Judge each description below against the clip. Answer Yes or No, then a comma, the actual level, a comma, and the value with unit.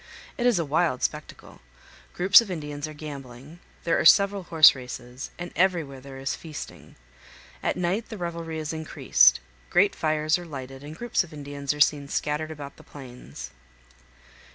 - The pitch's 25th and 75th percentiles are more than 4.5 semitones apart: No, average, 3.7 semitones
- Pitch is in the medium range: Yes, medium, 155 Hz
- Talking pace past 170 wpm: No, average, 165 wpm